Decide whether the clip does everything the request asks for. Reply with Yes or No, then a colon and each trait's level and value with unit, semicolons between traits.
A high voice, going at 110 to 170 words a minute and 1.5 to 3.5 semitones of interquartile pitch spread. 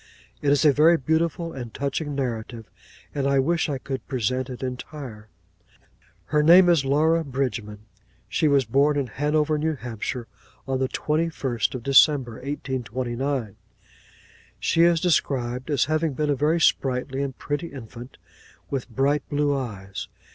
No: medium, 140 Hz; average, 150 wpm; average, 3.1 semitones